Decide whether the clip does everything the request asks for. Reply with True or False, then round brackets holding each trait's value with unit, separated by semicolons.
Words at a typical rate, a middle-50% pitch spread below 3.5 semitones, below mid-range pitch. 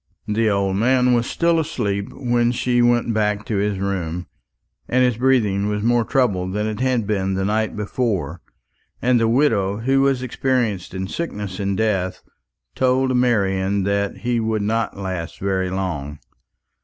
False (160 wpm; 3.9 semitones; 105 Hz)